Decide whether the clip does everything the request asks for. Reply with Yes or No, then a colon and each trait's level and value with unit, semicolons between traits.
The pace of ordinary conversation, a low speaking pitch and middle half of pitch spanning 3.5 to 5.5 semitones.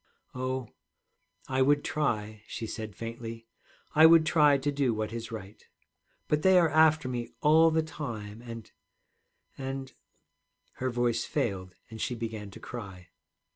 Yes: average, 150 wpm; low, 120 Hz; average, 4.8 semitones